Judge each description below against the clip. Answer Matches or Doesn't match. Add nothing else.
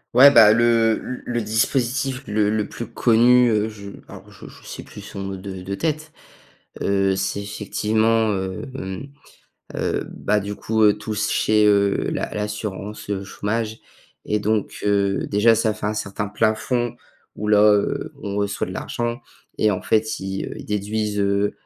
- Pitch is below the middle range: Matches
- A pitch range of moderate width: Doesn't match